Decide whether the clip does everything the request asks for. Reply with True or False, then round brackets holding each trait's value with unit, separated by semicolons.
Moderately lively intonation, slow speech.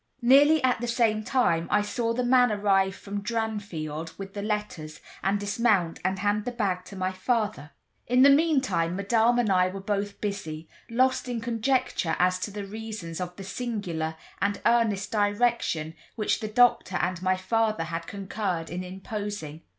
False (3.9 semitones; 170 wpm)